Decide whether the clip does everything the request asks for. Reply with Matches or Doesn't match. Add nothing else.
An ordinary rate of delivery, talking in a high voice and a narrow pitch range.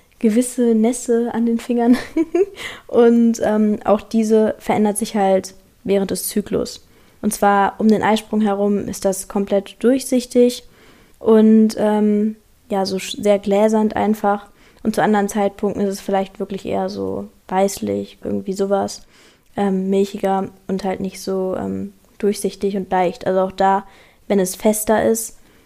Matches